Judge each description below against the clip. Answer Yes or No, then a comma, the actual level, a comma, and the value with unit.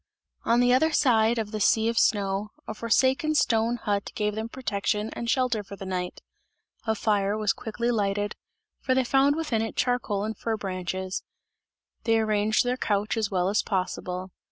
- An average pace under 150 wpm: No, average, 180 wpm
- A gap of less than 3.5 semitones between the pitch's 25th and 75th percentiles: Yes, average, 2.9 semitones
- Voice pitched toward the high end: Yes, high, 220 Hz